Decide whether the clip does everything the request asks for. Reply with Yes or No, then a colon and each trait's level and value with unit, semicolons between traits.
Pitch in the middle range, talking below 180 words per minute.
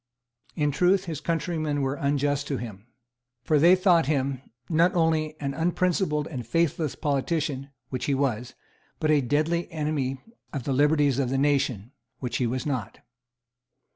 Yes: medium, 145 Hz; average, 155 wpm